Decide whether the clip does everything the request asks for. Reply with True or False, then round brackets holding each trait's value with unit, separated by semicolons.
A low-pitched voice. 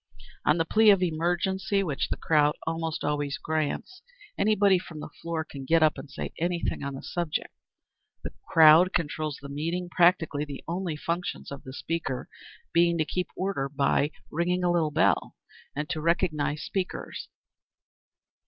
False (165 Hz)